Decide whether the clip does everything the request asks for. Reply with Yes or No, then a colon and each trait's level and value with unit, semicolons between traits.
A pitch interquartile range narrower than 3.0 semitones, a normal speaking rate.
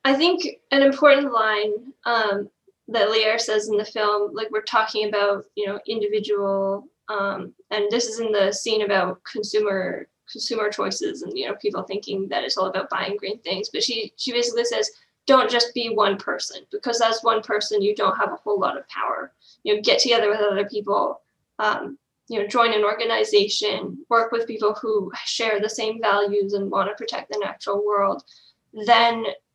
Yes: narrow, 2.5 semitones; average, 190 wpm